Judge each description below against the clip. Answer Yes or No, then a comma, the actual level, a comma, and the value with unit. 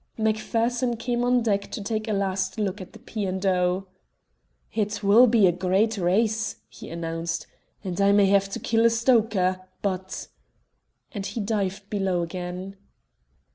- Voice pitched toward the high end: Yes, high, 200 Hz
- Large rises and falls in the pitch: No, average, 2.9 semitones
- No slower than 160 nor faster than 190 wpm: Yes, average, 170 wpm